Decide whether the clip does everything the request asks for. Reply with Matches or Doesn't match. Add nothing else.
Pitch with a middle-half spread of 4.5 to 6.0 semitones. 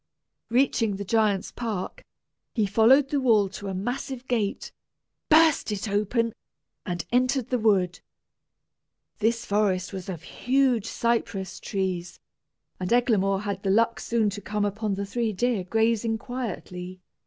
Doesn't match